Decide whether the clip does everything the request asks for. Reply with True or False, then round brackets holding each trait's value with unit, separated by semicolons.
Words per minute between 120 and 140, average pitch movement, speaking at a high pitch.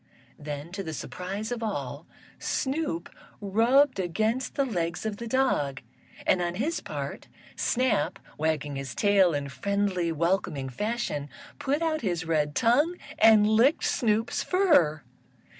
False (135 wpm; 7.0 semitones; 200 Hz)